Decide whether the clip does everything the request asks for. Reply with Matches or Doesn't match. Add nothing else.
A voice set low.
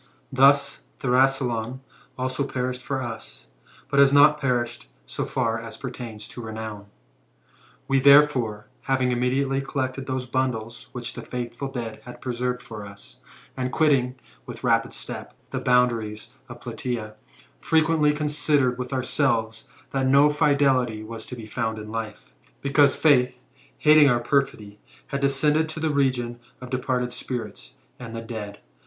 Matches